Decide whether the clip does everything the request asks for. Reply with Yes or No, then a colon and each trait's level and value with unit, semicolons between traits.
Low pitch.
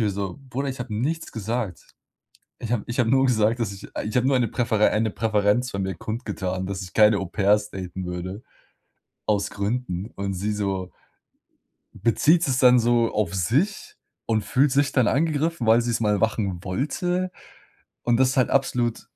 Yes: low, 110 Hz